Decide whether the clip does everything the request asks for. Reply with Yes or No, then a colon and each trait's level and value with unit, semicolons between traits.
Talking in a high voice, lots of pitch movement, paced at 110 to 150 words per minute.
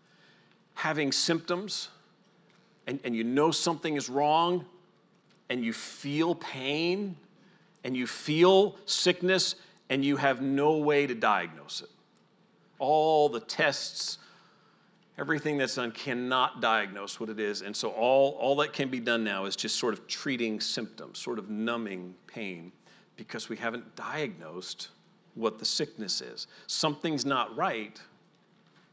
No: medium, 140 Hz; wide, 5.7 semitones; slow, 135 wpm